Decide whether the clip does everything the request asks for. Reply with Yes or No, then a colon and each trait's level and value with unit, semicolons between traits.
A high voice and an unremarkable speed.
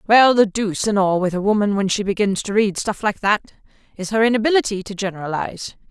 No: high, 205 Hz; fast, 215 wpm